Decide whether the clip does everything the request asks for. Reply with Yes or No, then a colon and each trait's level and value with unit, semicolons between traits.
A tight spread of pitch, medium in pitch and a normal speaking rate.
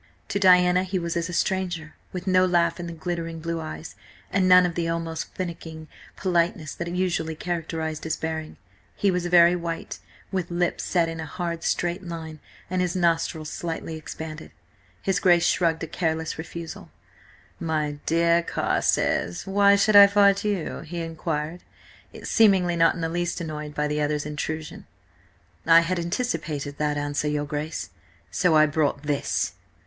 Yes: narrow, 2.1 semitones; medium, 170 Hz; average, 165 wpm